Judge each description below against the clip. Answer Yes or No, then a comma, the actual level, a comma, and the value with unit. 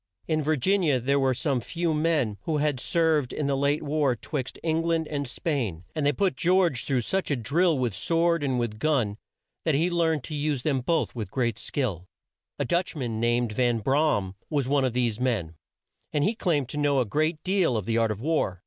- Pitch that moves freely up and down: No, average, 4.8 semitones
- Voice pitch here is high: No, medium, 140 Hz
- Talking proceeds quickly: Yes, fast, 225 wpm